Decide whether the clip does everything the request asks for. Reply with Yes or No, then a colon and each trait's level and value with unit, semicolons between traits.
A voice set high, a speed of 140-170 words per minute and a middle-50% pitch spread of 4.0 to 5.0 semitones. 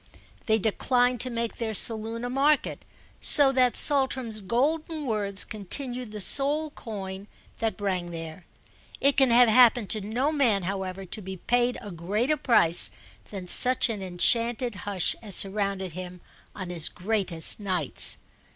Yes: high, 220 Hz; average, 150 wpm; average, 4.5 semitones